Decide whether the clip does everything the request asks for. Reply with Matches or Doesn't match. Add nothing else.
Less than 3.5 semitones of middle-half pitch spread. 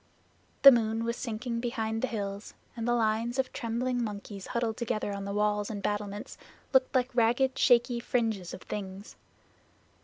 Matches